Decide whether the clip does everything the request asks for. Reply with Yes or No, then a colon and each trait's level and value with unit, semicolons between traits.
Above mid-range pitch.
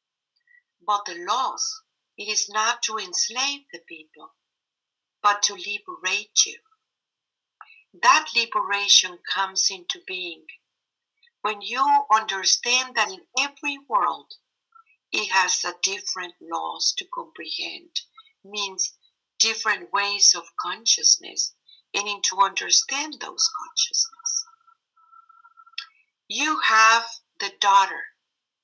Yes: very high, 265 Hz